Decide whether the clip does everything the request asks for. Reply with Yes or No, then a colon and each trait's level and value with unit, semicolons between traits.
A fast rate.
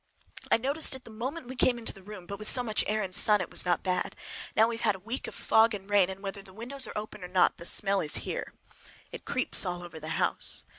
Yes: fast, 275 wpm